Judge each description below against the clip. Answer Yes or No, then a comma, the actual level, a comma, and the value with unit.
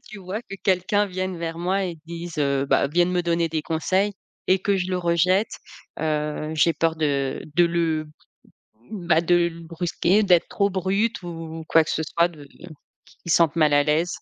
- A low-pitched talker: No, medium, 170 Hz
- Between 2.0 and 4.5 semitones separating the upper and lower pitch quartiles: Yes, narrow, 2.5 semitones